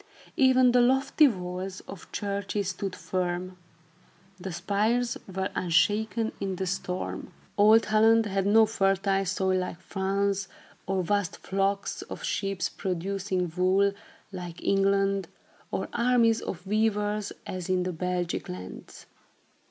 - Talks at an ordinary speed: No, slow, 125 wpm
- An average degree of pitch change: No, narrow, 2.3 semitones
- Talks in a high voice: Yes, high, 195 Hz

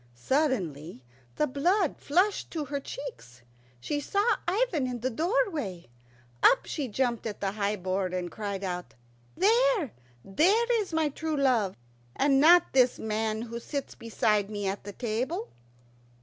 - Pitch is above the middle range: Yes, very high, 255 Hz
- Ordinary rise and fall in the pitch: No, wide, 7.9 semitones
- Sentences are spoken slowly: No, average, 150 wpm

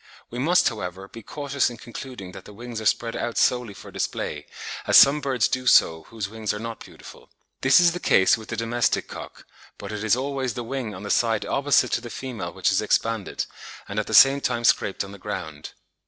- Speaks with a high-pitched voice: No, low, 115 Hz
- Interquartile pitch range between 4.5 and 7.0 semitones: No, average, 3.8 semitones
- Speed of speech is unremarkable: No, fast, 220 wpm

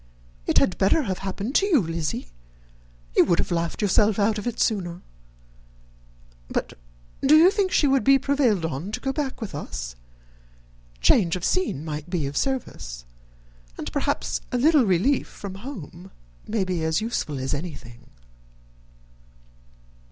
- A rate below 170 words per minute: Yes, average, 150 wpm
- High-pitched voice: Yes, high, 195 Hz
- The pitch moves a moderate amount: No, wide, 8.4 semitones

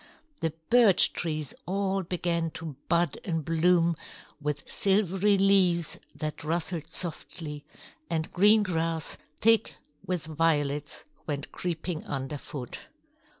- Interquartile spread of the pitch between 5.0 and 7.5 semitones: No, average, 3.2 semitones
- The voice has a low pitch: No, medium, 165 Hz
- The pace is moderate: No, slow, 105 wpm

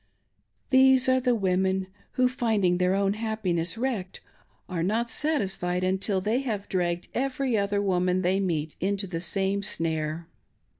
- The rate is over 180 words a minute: No, average, 150 wpm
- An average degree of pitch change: Yes, average, 3.9 semitones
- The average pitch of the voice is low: No, high, 195 Hz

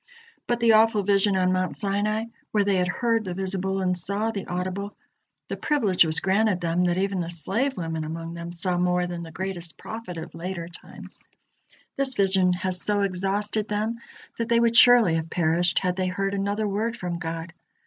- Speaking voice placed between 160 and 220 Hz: Yes, high, 190 Hz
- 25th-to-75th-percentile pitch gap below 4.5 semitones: Yes, average, 3.0 semitones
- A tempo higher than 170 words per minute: Yes, average, 190 wpm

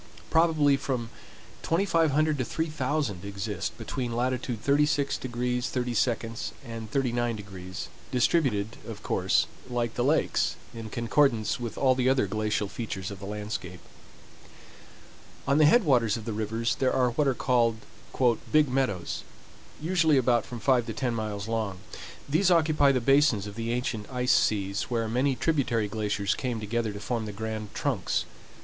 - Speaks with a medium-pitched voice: No, low, 120 Hz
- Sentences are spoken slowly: No, average, 150 wpm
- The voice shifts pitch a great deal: No, average, 4.0 semitones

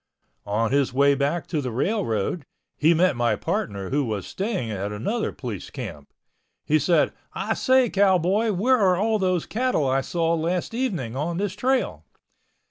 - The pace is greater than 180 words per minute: No, average, 165 wpm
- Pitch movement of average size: No, wide, 7.9 semitones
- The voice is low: No, medium, 165 Hz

